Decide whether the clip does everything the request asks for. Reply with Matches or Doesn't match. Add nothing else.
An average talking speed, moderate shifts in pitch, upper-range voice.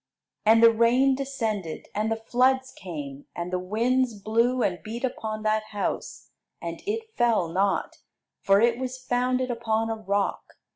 Matches